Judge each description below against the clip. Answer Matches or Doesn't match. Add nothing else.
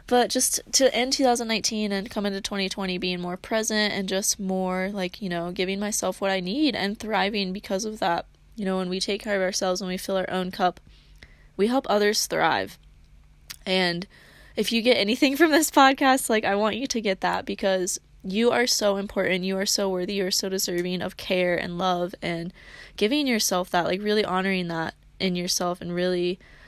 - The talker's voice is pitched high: Matches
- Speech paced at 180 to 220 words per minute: Matches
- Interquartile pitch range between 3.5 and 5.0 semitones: Doesn't match